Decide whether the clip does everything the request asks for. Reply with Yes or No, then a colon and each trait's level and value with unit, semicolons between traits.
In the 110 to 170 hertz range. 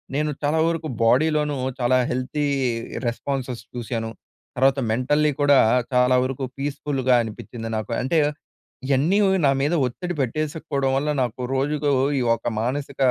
Yes: low, 135 Hz